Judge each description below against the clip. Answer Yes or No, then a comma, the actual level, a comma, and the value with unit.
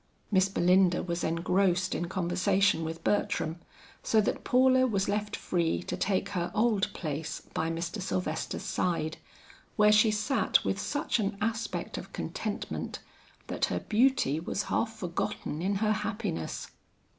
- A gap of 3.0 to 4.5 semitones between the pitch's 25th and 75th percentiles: Yes, average, 3.7 semitones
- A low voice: No, high, 190 Hz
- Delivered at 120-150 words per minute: Yes, average, 145 wpm